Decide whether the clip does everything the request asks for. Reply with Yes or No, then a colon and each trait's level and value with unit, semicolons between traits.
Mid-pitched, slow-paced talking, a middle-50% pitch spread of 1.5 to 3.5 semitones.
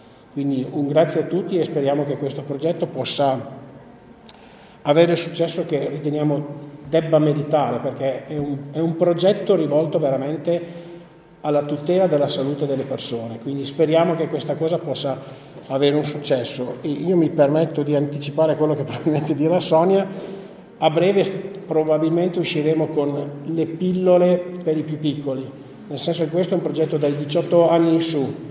No: medium, 155 Hz; average, 155 wpm; average, 2.9 semitones